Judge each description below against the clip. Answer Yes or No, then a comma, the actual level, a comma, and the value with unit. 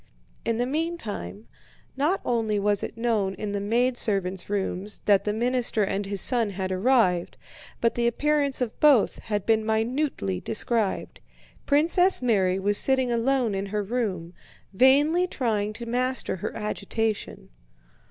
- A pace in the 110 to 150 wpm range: Yes, average, 140 wpm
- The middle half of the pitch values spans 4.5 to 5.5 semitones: No, average, 4.1 semitones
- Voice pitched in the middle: No, high, 225 Hz